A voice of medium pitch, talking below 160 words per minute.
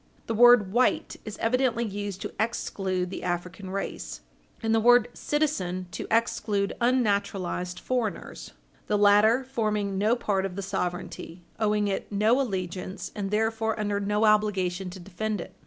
No: high, 205 Hz; average, 150 wpm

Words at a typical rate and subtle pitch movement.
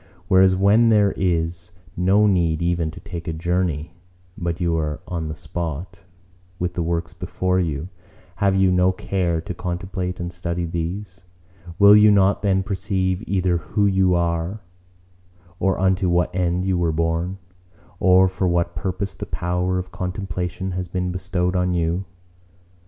Yes: average, 155 wpm; narrow, 1.7 semitones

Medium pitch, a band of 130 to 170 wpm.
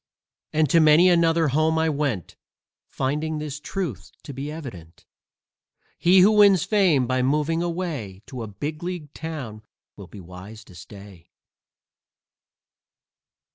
Yes: medium, 150 Hz; slow, 135 wpm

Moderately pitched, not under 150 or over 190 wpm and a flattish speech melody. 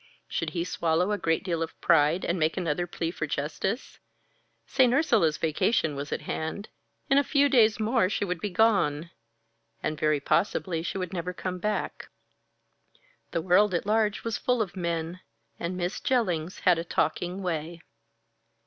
No: medium, 180 Hz; average, 165 wpm; average, 4.3 semitones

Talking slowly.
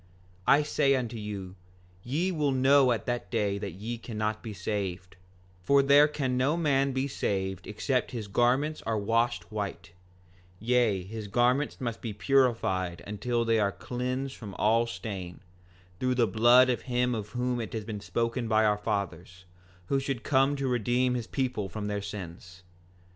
No: average, 170 wpm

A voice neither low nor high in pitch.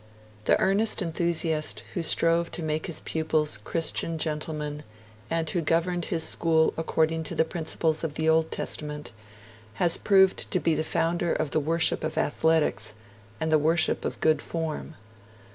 Yes: medium, 160 Hz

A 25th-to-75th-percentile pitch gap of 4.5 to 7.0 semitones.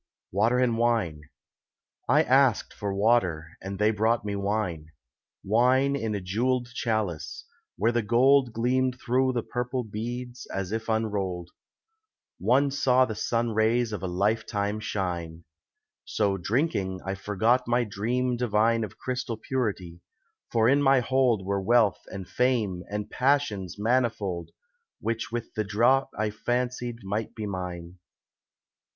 No: average, 3.8 semitones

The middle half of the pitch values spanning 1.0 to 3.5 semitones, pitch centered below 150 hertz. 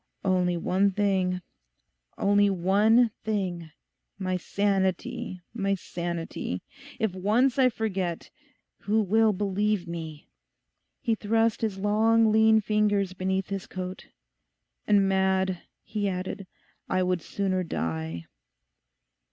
No: narrow, 2.5 semitones; high, 195 Hz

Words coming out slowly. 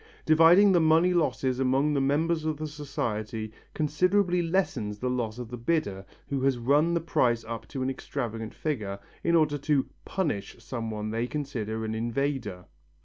No: average, 170 wpm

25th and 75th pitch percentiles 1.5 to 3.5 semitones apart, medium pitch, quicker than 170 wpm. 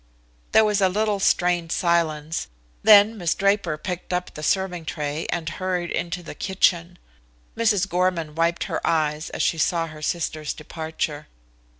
No: average, 3.0 semitones; medium, 175 Hz; average, 155 wpm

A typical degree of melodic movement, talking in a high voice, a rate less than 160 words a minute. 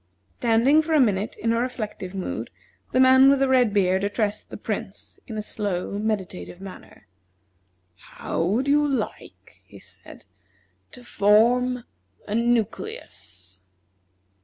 Yes: average, 4.1 semitones; high, 225 Hz; slow, 135 wpm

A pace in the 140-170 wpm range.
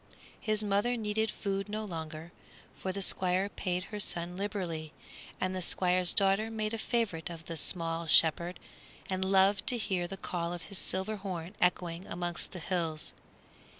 Yes: average, 165 wpm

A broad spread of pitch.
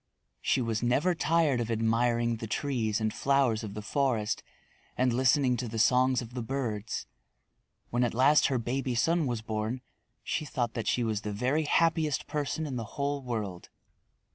No: average, 3.5 semitones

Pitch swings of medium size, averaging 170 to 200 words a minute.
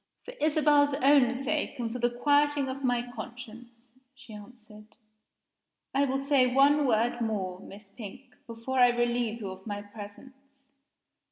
No: average, 3.5 semitones; average, 150 wpm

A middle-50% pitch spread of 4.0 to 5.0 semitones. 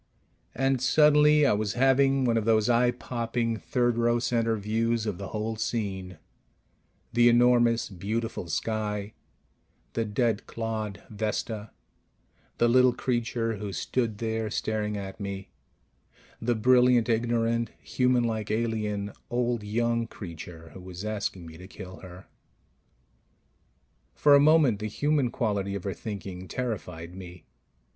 No: average, 2.8 semitones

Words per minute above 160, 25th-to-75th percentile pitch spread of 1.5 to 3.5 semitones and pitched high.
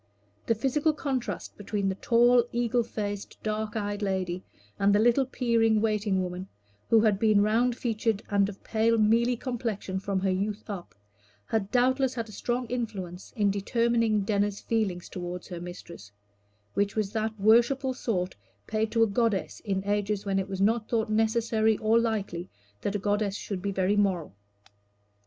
Yes: average, 170 wpm; average, 2.7 semitones; high, 215 Hz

